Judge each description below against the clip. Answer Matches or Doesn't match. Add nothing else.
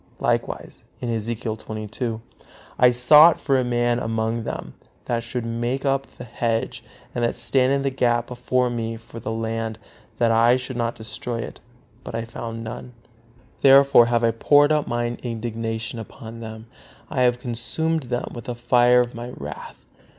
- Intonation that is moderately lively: Doesn't match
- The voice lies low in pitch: Matches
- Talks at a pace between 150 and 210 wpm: Matches